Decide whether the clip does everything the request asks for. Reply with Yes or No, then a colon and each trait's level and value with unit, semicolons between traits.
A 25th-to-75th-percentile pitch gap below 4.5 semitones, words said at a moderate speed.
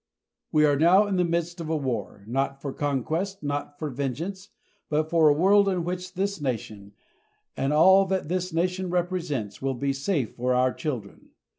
No: average, 5.1 semitones; average, 180 wpm